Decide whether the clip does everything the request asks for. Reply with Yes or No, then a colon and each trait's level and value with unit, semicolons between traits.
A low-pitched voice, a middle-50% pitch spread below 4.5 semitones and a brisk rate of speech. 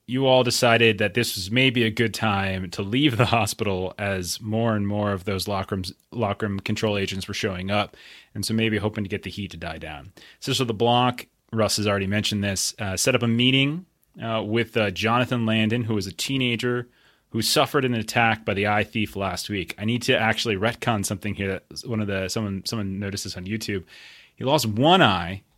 Yes: low, 110 Hz; average, 3.1 semitones; fast, 225 wpm